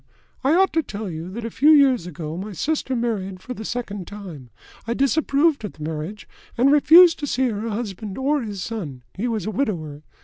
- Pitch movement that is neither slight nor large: No, wide, 6.5 semitones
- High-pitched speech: Yes, high, 220 Hz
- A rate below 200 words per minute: No, fast, 205 wpm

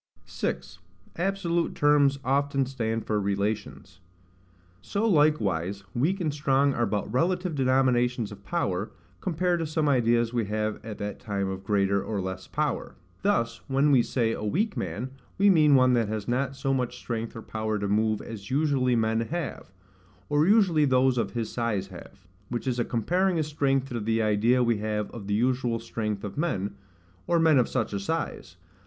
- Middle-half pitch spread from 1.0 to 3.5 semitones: No, wide, 5.4 semitones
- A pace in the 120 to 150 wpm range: No, average, 180 wpm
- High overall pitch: No, low, 120 Hz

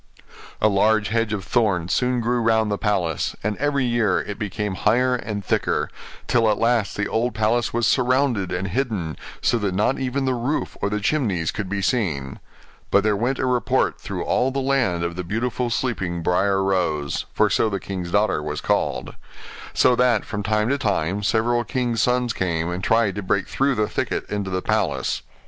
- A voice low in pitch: Yes, low, 105 Hz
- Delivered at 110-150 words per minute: No, average, 195 wpm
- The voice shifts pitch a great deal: No, average, 4.1 semitones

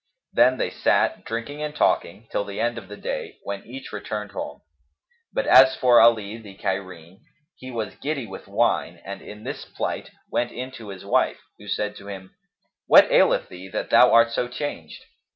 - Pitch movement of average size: Yes, average, 3.6 semitones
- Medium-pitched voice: No, low, 105 Hz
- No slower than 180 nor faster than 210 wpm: Yes, average, 190 wpm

